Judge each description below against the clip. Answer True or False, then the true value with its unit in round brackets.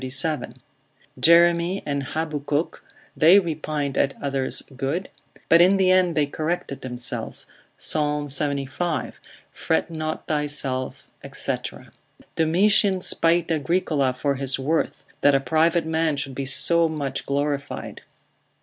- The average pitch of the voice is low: False (150 Hz)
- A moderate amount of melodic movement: True (3.3 semitones)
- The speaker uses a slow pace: True (120 wpm)